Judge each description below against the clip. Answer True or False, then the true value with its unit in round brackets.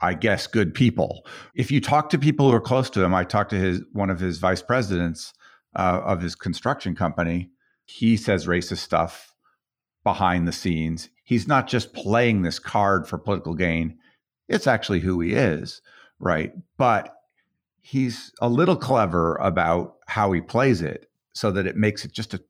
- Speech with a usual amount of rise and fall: False (5.7 semitones)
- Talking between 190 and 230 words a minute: False (180 wpm)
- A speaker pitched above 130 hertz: False (100 Hz)